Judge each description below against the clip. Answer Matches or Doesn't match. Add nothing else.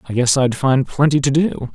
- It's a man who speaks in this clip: Matches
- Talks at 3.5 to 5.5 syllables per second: Matches